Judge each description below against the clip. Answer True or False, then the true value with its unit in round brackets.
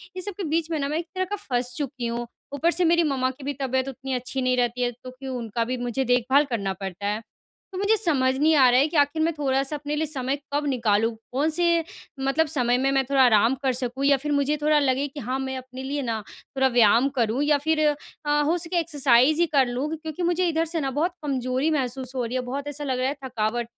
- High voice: True (270 Hz)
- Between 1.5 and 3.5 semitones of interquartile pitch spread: True (3.2 semitones)